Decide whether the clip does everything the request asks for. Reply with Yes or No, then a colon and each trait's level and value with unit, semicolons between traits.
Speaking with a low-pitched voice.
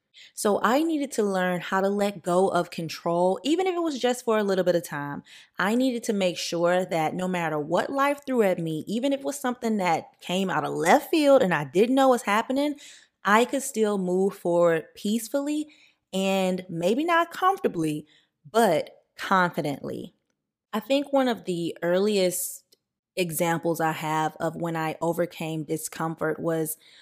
No: high, 190 Hz